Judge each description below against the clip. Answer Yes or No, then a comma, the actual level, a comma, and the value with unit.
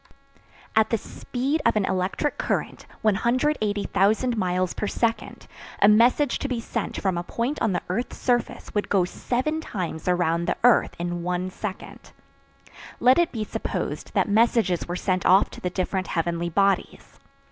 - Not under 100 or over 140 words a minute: No, average, 160 wpm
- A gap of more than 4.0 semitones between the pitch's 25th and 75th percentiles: Yes, average, 4.8 semitones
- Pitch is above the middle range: Yes, high, 205 Hz